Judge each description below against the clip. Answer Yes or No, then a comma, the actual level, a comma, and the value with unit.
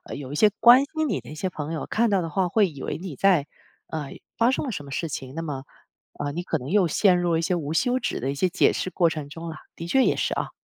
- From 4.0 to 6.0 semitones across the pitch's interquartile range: Yes, average, 5.0 semitones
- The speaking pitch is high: No, medium, 170 Hz